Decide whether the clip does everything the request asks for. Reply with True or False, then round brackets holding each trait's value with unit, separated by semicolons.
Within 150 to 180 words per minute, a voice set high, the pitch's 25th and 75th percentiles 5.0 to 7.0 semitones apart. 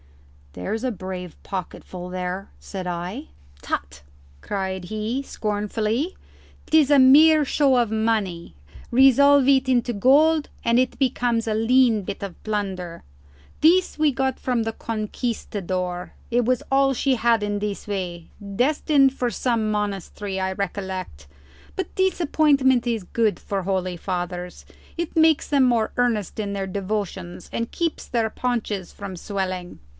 False (140 wpm; 220 Hz; 5.5 semitones)